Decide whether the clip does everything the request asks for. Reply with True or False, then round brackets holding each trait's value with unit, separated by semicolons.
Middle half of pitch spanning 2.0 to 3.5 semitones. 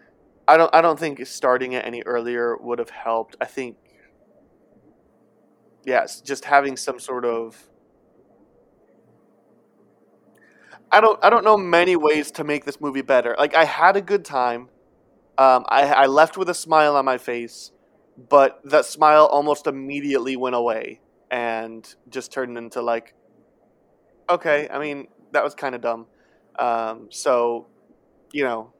False (4.1 semitones)